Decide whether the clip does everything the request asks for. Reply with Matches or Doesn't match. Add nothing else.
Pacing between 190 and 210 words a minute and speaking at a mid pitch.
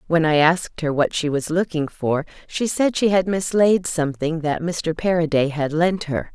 Matches